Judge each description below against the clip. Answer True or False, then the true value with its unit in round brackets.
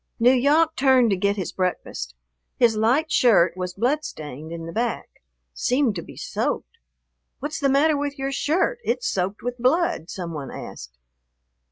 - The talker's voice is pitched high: True (240 Hz)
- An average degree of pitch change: False (7.8 semitones)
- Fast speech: False (165 wpm)